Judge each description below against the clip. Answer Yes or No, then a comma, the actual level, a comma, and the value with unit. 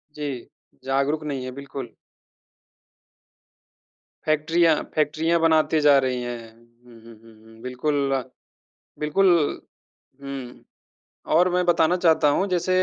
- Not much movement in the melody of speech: No, average, 4.3 semitones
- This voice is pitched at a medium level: Yes, medium, 145 Hz